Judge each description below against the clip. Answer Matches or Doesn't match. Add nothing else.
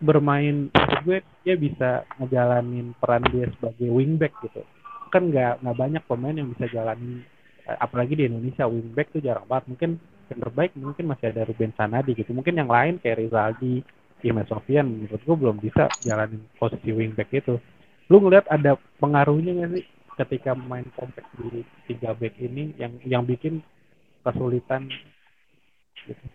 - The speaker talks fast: Matches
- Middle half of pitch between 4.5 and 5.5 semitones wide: Doesn't match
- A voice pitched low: Matches